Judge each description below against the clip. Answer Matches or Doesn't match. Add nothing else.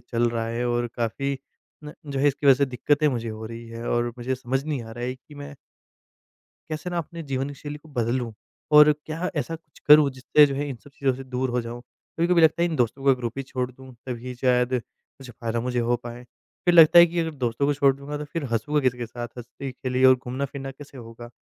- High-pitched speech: Doesn't match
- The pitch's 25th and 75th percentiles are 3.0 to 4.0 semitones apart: Matches